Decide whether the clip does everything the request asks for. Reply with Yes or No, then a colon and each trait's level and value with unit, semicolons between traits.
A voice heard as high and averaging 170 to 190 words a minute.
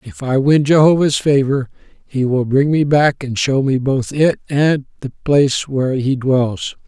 No: low, 135 Hz; average, 185 wpm